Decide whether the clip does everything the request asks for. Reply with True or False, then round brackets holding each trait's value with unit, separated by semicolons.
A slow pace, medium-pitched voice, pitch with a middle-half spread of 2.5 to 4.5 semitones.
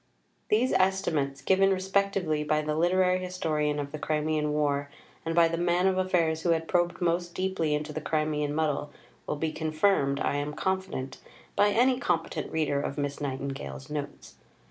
False (165 wpm; 160 Hz; 3.7 semitones)